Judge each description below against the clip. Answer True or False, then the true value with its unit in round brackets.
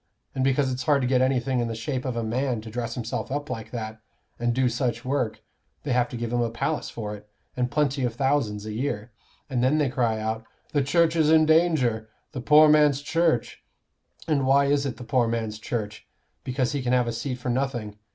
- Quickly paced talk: True (225 wpm)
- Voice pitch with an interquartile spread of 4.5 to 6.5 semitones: False (3.3 semitones)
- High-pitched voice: False (125 Hz)